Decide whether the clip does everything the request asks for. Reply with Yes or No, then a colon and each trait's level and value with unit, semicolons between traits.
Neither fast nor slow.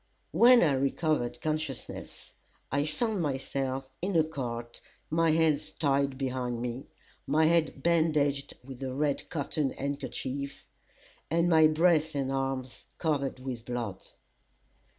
No: slow, 125 wpm